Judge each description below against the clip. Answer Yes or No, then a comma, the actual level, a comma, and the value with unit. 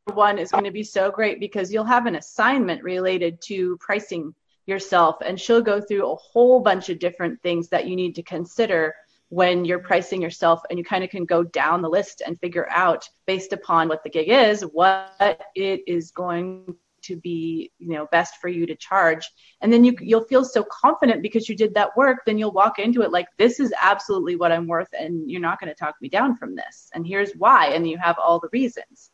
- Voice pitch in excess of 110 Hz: Yes, medium, 185 Hz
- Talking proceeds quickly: Yes, fast, 225 wpm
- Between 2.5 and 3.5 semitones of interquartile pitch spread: No, average, 3.9 semitones